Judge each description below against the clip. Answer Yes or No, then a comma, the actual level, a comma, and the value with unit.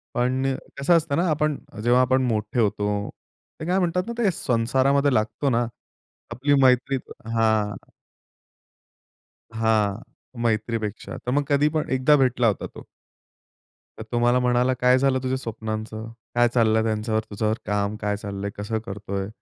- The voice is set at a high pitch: No, low, 120 Hz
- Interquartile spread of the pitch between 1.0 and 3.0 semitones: No, average, 3.5 semitones